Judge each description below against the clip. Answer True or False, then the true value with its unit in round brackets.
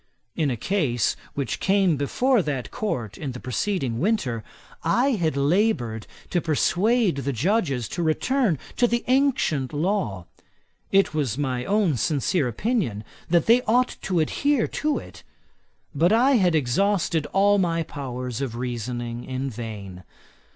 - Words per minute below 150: True (140 wpm)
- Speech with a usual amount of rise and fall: False (8.4 semitones)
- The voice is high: False (155 Hz)